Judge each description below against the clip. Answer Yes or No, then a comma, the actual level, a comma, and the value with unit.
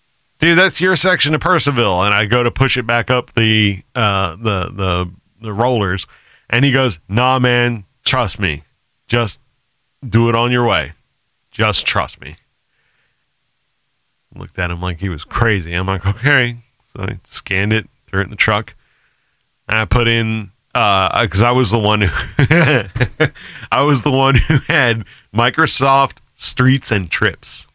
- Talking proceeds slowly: No, average, 165 wpm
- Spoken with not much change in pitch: No, average, 4.5 semitones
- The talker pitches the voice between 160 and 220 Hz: No, low, 120 Hz